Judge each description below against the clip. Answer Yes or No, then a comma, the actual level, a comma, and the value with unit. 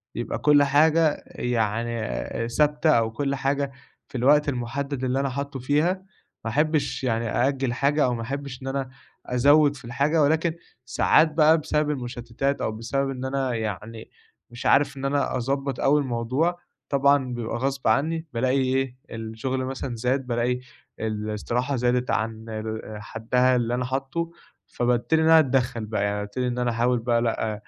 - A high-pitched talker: No, low, 130 Hz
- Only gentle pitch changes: No, average, 3.2 semitones